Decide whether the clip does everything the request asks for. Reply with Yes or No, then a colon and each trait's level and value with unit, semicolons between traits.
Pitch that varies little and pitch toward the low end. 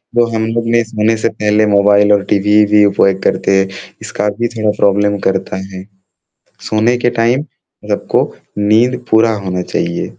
Yes: narrow, 2.1 semitones; low, 105 Hz